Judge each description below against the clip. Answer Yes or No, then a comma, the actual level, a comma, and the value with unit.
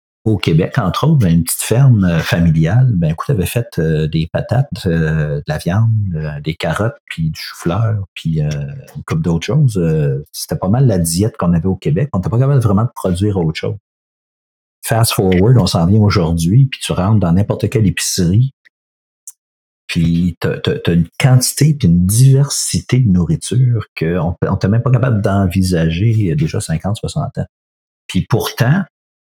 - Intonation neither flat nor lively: No, wide, 6.6 semitones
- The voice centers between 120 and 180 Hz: No, very low, 95 Hz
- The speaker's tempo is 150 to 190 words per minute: Yes, average, 185 wpm